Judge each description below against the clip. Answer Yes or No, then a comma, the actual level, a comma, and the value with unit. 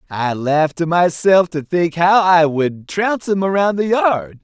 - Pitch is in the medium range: Yes, medium, 170 Hz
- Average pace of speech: Yes, average, 190 wpm